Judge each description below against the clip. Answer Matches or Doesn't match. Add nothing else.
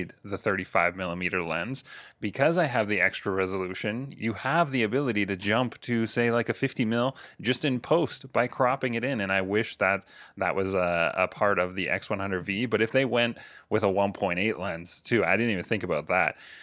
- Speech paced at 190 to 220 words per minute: Matches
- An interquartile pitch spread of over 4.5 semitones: Doesn't match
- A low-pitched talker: Matches